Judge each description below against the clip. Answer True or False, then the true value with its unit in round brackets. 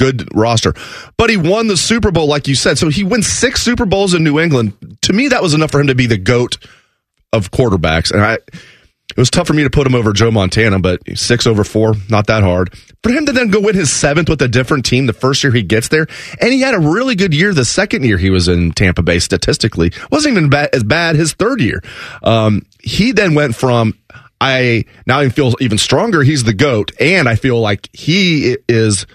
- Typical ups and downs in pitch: False (6.6 semitones)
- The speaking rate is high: True (235 wpm)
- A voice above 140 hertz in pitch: False (130 Hz)